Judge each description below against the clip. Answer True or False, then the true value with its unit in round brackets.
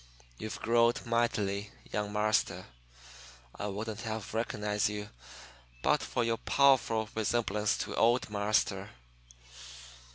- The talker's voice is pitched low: True (110 Hz)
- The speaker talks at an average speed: False (105 wpm)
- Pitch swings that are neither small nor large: False (2.0 semitones)